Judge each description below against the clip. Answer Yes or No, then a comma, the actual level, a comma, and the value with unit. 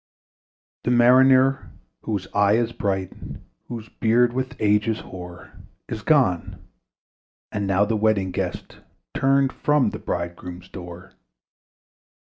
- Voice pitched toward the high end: No, low, 110 Hz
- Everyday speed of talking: No, slow, 120 wpm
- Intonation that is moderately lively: Yes, average, 4.6 semitones